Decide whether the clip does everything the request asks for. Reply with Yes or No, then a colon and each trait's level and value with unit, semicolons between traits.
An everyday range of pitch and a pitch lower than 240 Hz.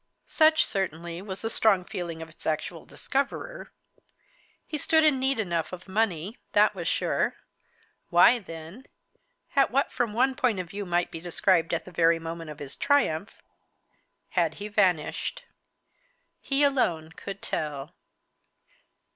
No: wide, 6.6 semitones; medium, 185 Hz